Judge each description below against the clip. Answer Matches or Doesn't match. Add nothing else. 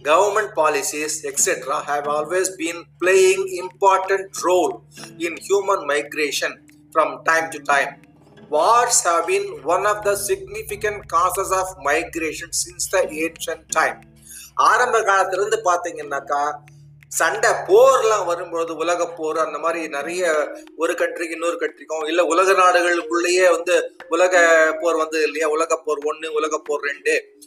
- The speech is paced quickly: Doesn't match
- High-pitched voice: Doesn't match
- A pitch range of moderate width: Matches